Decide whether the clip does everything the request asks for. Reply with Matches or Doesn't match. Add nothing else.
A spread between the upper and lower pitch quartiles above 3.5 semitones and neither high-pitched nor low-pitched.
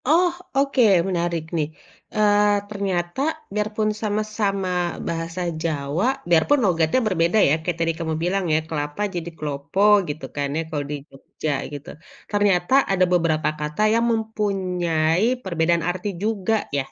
Matches